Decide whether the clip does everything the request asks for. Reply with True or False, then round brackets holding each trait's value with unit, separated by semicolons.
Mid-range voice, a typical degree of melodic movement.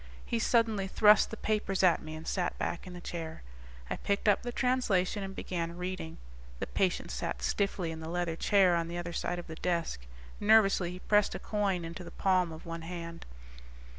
True (180 Hz; 3.1 semitones)